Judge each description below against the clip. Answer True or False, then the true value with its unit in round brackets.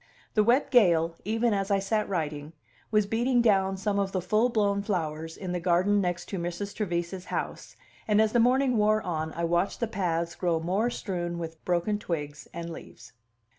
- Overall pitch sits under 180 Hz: False (190 Hz)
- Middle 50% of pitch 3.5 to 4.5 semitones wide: True (3.8 semitones)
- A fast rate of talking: False (185 wpm)